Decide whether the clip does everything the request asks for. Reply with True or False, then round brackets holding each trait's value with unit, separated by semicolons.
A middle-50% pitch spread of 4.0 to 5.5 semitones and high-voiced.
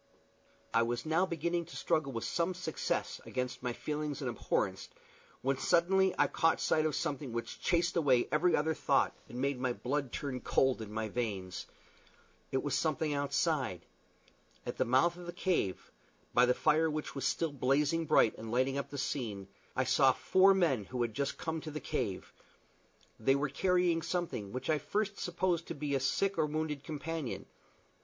False (4.6 semitones; 145 Hz)